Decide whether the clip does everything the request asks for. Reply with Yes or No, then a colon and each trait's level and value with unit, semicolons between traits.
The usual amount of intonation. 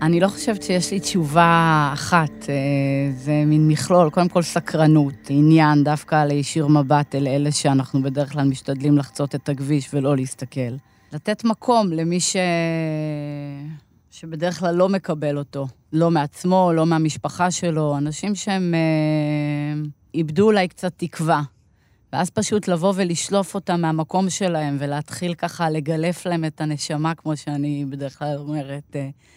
Yes: average, 3.3 semitones